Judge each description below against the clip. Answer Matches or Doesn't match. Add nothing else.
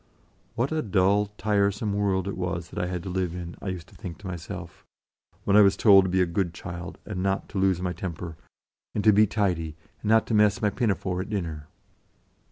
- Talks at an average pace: Doesn't match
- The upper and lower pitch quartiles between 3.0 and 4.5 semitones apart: Doesn't match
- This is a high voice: Doesn't match